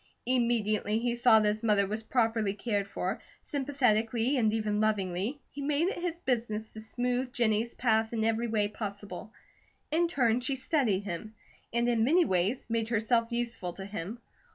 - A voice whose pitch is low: No, high, 225 Hz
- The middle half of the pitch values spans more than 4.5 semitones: No, average, 2.7 semitones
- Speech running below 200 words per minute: Yes, average, 170 wpm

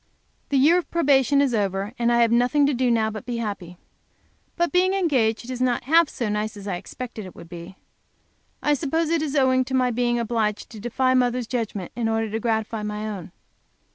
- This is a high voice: Yes, high, 240 Hz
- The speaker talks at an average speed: No, fast, 215 wpm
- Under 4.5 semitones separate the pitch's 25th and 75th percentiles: Yes, average, 3.7 semitones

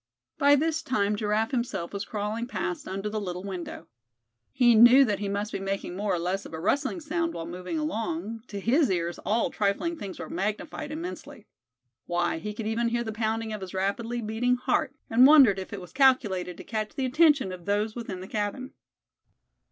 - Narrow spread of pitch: No, average, 4.4 semitones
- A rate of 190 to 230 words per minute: Yes, average, 200 wpm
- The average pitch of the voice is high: Yes, high, 215 Hz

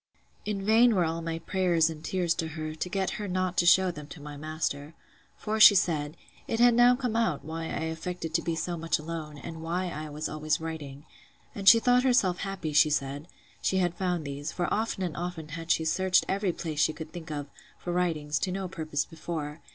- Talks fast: Yes, fast, 220 wpm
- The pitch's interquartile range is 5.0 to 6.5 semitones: No, average, 3.2 semitones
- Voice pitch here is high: No, medium, 165 Hz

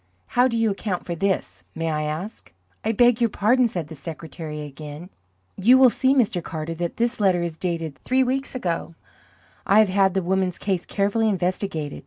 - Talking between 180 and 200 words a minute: Yes, average, 190 wpm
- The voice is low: No, high, 190 Hz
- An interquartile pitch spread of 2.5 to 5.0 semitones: No, wide, 5.4 semitones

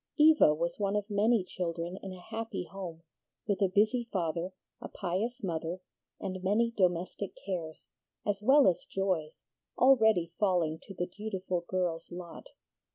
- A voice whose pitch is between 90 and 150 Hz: No, medium, 185 Hz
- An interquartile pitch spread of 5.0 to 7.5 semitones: No, average, 3.3 semitones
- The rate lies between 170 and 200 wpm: No, average, 150 wpm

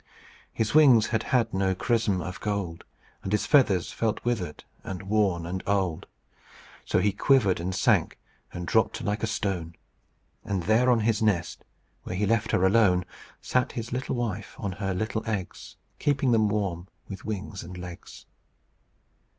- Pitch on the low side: Yes, low, 100 Hz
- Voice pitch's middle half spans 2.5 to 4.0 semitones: Yes, average, 3.5 semitones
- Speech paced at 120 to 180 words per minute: Yes, average, 160 wpm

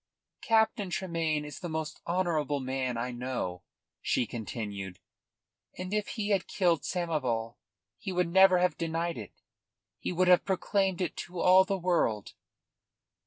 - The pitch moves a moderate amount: No, wide, 6.2 semitones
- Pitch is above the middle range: No, medium, 170 Hz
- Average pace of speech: Yes, average, 145 wpm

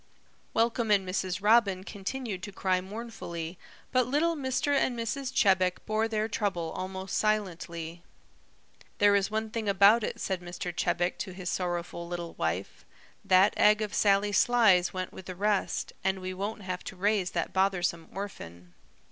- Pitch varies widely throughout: No, average, 3.1 semitones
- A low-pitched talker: No, high, 195 Hz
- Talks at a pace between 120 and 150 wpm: No, average, 160 wpm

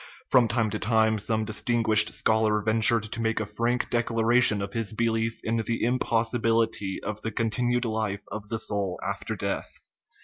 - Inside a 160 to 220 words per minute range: Yes, average, 175 wpm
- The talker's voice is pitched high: No, low, 110 Hz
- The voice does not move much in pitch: Yes, narrow, 1.3 semitones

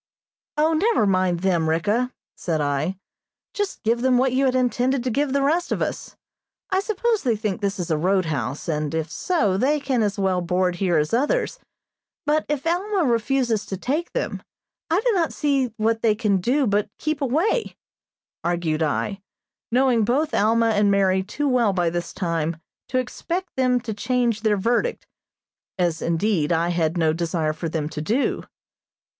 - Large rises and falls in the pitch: Yes, wide, 7.5 semitones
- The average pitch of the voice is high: Yes, high, 220 Hz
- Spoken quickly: No, average, 175 wpm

